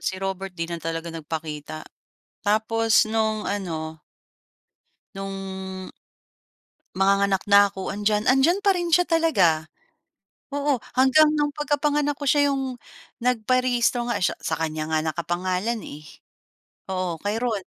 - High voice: Yes, high, 205 Hz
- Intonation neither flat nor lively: No, wide, 6.5 semitones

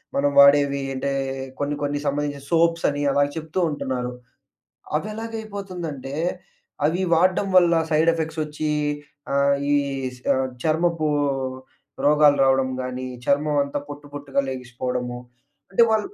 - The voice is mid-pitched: Yes, medium, 145 Hz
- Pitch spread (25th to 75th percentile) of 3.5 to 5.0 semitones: No, average, 2.9 semitones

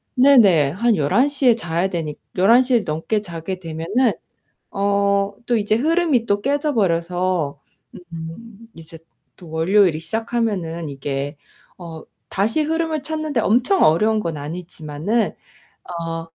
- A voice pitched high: Yes, high, 200 Hz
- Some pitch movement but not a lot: No, wide, 6.3 semitones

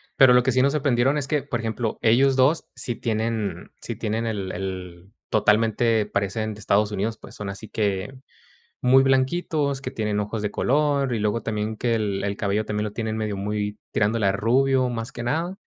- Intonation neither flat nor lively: Yes, average, 3.8 semitones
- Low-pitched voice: Yes, low, 110 Hz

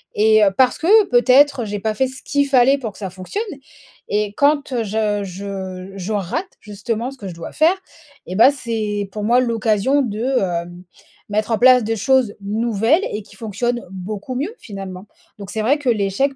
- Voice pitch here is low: No, high, 220 Hz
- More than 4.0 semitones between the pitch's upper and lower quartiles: Yes, average, 4.4 semitones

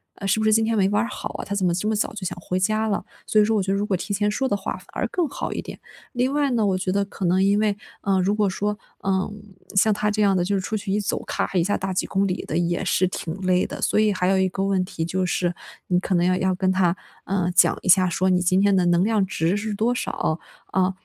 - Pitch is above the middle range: Yes, high, 195 Hz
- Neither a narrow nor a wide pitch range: No, narrow, 2.2 semitones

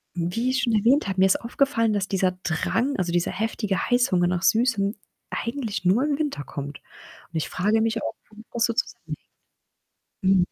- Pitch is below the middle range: No, high, 215 Hz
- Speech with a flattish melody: No, average, 4.3 semitones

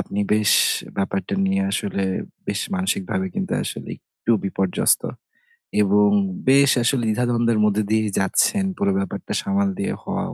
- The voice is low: Yes, low, 110 Hz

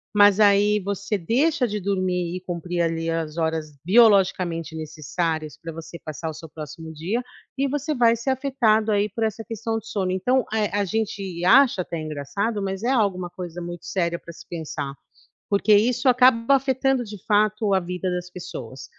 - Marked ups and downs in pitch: No, average, 4.7 semitones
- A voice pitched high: Yes, high, 195 Hz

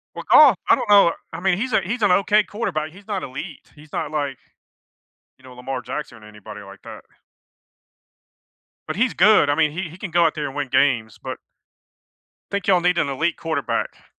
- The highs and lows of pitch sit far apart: Yes, wide, 6.4 semitones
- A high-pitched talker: No, medium, 160 Hz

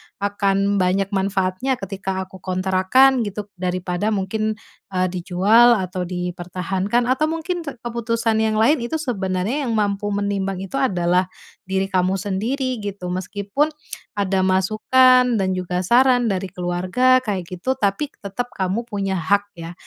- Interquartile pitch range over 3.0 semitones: Yes, average, 4.1 semitones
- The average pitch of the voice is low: No, high, 200 Hz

